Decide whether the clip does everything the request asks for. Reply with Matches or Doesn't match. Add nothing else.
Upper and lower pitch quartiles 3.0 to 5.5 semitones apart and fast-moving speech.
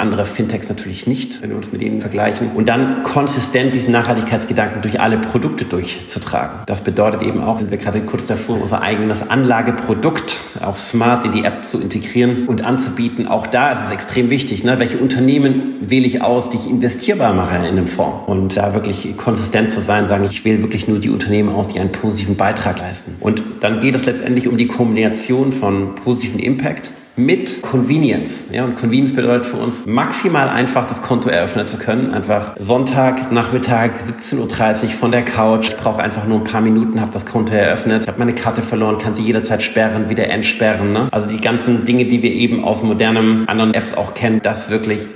Doesn't match